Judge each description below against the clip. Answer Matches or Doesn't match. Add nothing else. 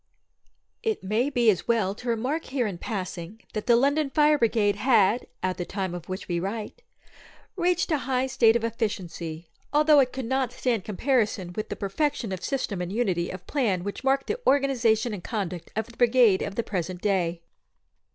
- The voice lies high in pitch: Matches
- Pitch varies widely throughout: Matches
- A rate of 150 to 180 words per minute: Doesn't match